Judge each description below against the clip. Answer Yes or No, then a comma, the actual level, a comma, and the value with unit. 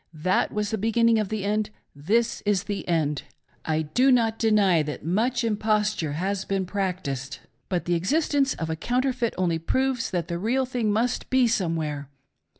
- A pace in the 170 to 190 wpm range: Yes, average, 180 wpm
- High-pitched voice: Yes, high, 205 Hz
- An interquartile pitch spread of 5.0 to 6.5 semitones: Yes, average, 5.3 semitones